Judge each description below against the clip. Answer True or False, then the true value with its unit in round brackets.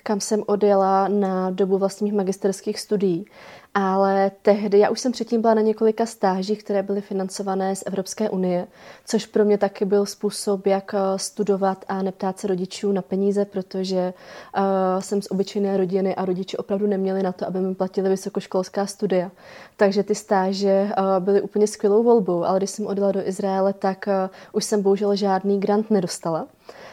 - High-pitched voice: True (195 Hz)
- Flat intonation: True (1.3 semitones)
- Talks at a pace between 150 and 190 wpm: True (170 wpm)